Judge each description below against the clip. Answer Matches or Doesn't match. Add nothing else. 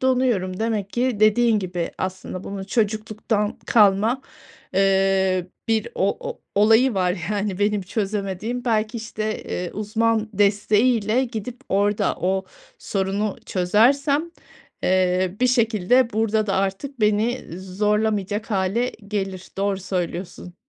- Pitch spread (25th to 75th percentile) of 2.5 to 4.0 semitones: Matches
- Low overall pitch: Doesn't match